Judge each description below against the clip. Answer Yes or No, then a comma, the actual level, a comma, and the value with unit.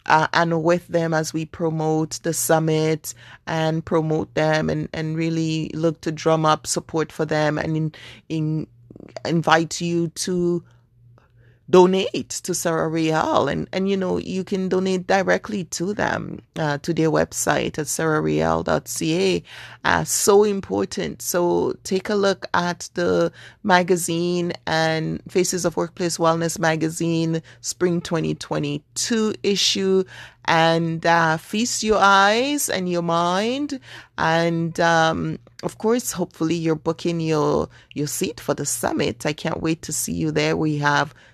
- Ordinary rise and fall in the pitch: No, narrow, 2.3 semitones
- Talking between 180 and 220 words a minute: No, average, 140 wpm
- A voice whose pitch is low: No, medium, 165 Hz